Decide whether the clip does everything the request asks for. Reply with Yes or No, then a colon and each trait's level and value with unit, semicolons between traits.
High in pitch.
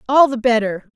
Yes: high, 240 Hz